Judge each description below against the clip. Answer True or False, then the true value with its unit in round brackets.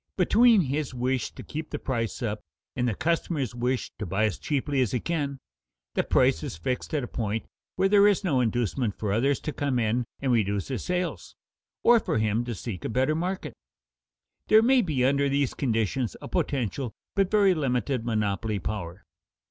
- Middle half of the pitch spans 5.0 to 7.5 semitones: True (5.6 semitones)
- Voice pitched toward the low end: True (130 Hz)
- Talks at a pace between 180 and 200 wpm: True (190 wpm)